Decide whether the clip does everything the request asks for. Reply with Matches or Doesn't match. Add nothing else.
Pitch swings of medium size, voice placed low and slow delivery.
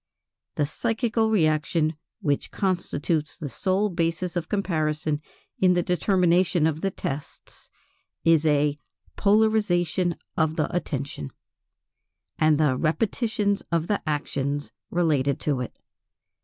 Doesn't match